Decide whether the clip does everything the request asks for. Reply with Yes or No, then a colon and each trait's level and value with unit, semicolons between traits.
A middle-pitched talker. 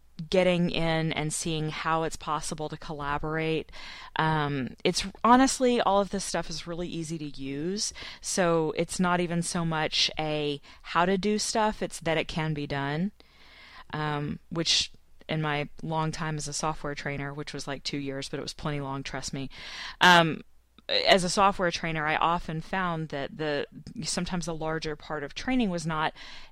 Yes: medium, 160 Hz